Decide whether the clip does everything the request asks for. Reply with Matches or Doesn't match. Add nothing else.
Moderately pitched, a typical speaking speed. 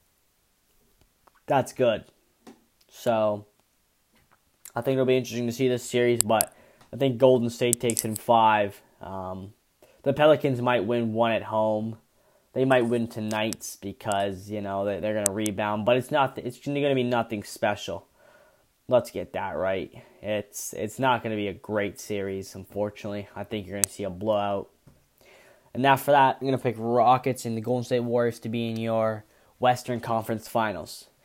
Doesn't match